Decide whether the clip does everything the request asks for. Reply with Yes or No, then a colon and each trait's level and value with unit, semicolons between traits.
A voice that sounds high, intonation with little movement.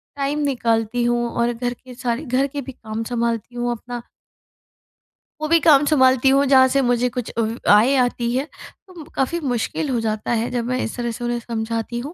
Yes: high, 245 Hz; narrow, 2.3 semitones